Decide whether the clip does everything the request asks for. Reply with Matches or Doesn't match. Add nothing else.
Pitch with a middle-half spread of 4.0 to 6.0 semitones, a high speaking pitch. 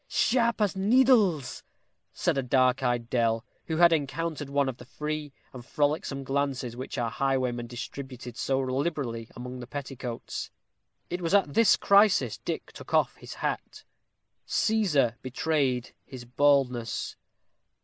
Doesn't match